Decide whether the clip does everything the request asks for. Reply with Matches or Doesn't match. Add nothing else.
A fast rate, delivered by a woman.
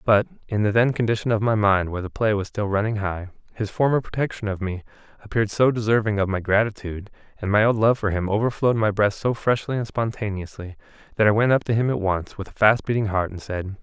Doesn't match